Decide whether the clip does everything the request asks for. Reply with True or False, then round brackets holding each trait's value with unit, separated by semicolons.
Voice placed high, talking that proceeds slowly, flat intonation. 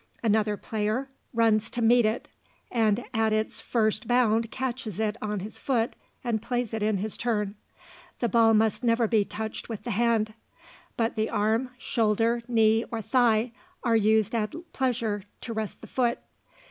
False (225 Hz; 160 wpm; 1.7 semitones)